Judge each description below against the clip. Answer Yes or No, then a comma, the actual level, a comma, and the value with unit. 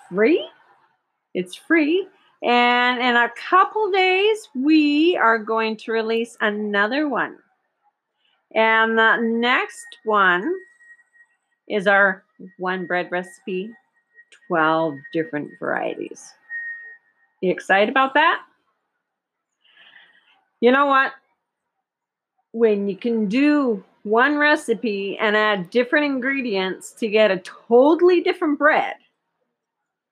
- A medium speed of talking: No, slow, 100 wpm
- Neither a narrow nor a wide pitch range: No, wide, 8.3 semitones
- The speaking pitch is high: Yes, high, 240 Hz